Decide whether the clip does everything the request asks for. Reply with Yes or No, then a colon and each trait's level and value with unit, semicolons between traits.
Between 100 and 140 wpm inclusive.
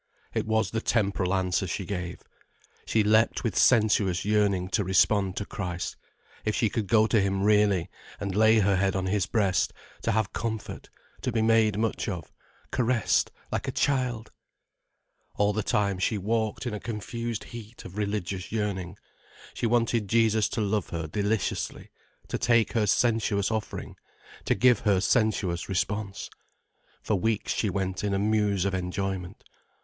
No: average, 160 wpm